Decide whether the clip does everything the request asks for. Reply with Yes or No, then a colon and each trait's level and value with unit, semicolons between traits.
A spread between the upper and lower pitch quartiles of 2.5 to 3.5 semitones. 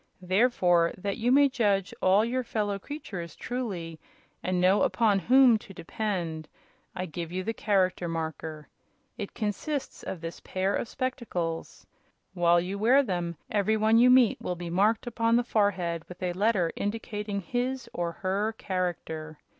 No: average, 4.5 semitones